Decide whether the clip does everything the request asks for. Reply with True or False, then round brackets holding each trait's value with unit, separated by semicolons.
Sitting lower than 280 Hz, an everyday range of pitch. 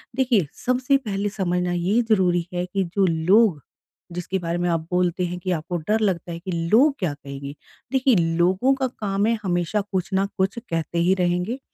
True (185 Hz; 3.6 semitones)